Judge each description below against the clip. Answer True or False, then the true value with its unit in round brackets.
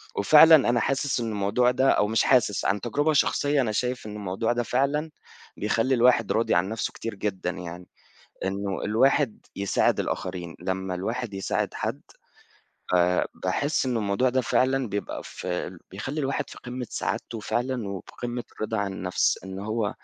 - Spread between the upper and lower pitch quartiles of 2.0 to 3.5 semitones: False (4.5 semitones)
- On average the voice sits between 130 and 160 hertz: False (110 Hz)